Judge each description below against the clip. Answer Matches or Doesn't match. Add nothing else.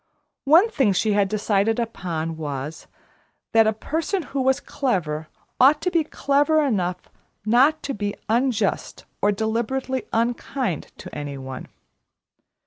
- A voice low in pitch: Doesn't match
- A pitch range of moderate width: Doesn't match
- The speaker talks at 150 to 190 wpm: Doesn't match